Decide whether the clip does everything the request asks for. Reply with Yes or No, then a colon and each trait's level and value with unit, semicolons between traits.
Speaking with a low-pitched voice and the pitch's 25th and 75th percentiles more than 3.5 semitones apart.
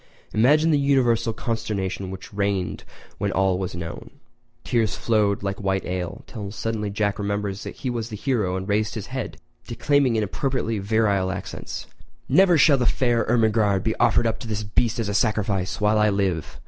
No: low, 105 Hz; average, 2.9 semitones